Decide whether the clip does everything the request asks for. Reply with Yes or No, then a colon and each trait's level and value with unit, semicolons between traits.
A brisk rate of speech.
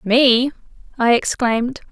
No: slow, 95 wpm